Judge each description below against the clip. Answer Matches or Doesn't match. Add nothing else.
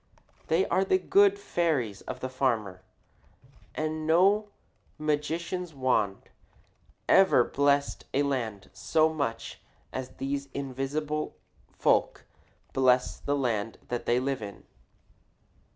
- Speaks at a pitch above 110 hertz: Matches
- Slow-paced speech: Matches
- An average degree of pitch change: Matches